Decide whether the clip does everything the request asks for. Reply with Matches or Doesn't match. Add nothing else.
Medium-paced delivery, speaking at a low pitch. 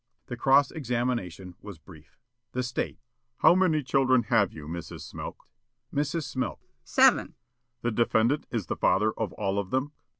Matches